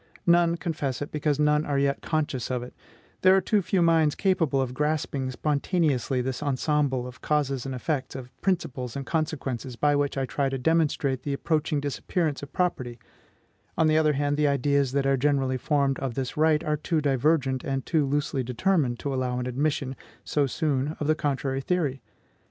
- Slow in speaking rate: No, average, 185 wpm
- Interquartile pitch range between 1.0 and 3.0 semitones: Yes, average, 2.7 semitones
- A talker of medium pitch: Yes, medium, 145 Hz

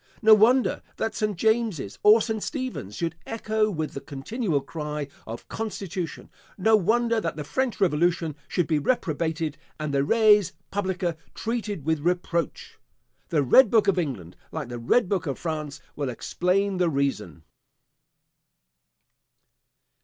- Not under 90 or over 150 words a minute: Yes, average, 140 wpm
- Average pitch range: No, wide, 6.4 semitones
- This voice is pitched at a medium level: Yes, medium, 175 Hz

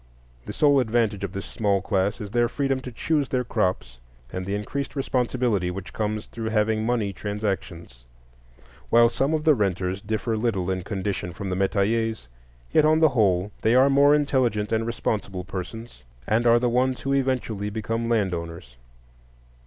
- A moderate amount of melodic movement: Yes, average, 4.0 semitones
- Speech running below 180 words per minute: Yes, average, 170 wpm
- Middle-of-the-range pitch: No, low, 110 Hz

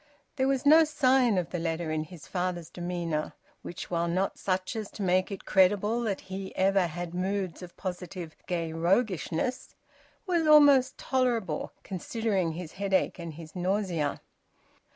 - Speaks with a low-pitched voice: No, medium, 185 Hz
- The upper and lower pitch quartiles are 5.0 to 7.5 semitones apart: No, average, 4.2 semitones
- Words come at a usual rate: Yes, average, 150 wpm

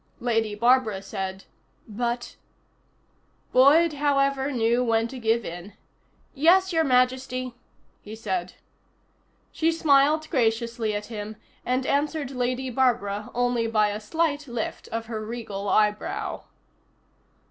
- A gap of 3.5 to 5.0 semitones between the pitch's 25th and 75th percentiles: Yes, average, 4.1 semitones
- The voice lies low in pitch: No, high, 240 Hz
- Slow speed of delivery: Yes, slow, 120 wpm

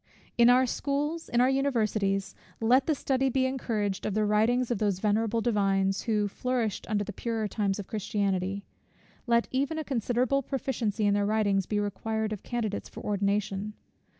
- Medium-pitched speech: No, high, 220 Hz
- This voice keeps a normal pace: Yes, average, 170 wpm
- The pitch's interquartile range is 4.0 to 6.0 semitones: No, average, 3.5 semitones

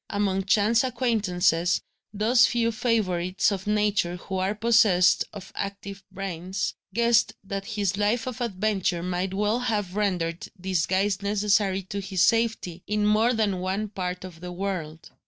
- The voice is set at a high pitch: Yes, high, 200 Hz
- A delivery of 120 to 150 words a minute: Yes, average, 145 wpm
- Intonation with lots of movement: No, narrow, 2.6 semitones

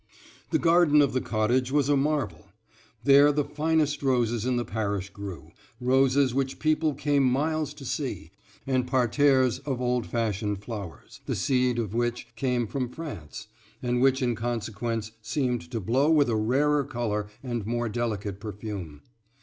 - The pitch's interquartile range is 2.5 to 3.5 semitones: No, average, 4.0 semitones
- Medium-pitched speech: No, low, 125 Hz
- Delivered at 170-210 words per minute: No, average, 155 wpm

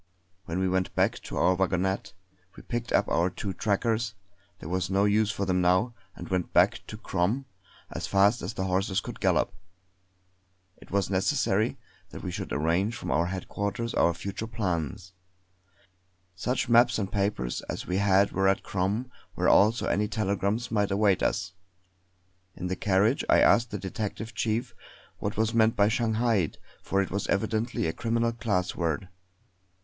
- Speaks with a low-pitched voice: Yes, low, 100 Hz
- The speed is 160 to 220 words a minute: Yes, average, 165 wpm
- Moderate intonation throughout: Yes, average, 3.2 semitones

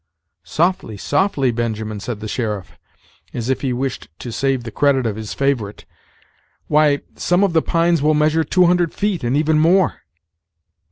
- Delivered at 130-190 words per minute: Yes, average, 165 wpm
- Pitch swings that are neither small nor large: No, wide, 6.0 semitones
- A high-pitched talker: No, medium, 140 Hz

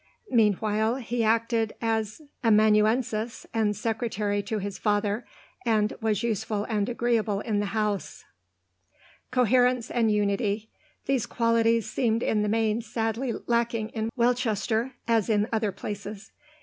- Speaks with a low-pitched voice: No, high, 220 Hz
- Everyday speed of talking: No, slow, 125 wpm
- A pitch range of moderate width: No, narrow, 1.7 semitones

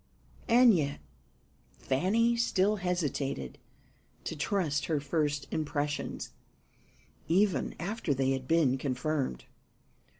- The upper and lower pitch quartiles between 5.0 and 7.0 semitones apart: Yes, average, 5.3 semitones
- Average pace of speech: No, slow, 95 wpm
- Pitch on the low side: No, medium, 155 Hz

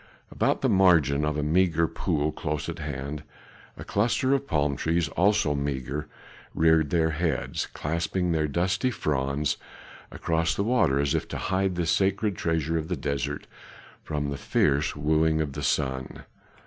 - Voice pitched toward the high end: No, very low, 80 Hz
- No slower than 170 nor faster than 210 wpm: No, average, 160 wpm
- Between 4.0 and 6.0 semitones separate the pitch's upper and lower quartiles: No, average, 3.1 semitones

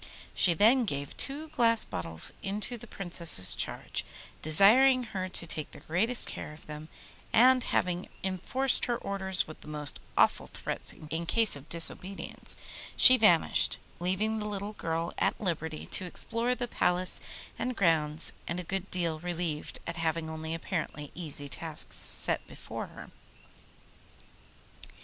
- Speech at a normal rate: Yes, average, 145 wpm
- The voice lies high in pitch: No, medium, 180 Hz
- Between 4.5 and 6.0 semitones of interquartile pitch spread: Yes, average, 5.3 semitones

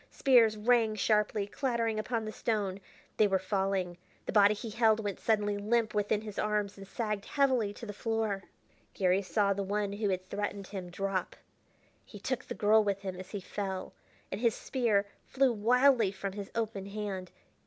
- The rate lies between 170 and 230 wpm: Yes, average, 180 wpm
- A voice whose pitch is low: No, high, 210 Hz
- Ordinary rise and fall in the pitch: No, narrow, 2.1 semitones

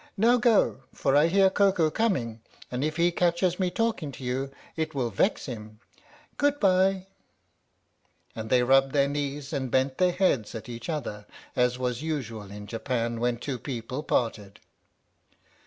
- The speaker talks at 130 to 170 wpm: Yes, average, 165 wpm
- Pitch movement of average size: No, wide, 6.6 semitones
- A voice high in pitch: No, low, 135 Hz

